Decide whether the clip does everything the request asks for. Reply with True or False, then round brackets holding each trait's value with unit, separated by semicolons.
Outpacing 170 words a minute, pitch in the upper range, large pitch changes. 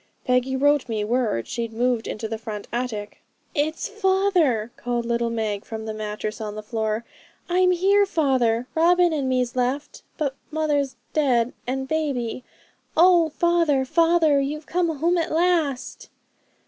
False (150 wpm; 265 Hz; 5.7 semitones)